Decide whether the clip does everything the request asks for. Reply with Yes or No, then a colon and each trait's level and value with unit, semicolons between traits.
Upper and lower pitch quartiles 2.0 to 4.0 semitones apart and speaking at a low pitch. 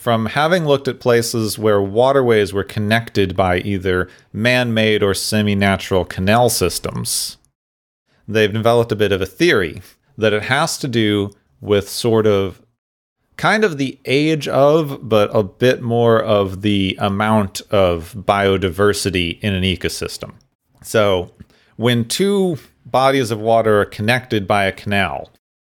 Yes: average, 3.4 semitones; low, 105 Hz